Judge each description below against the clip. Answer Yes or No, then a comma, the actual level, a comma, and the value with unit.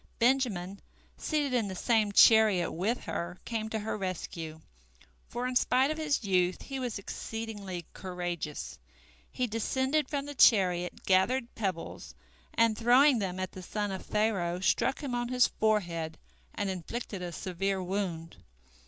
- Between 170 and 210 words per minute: No, average, 150 wpm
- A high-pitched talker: Yes, high, 210 Hz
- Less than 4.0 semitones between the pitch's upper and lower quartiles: No, average, 5.0 semitones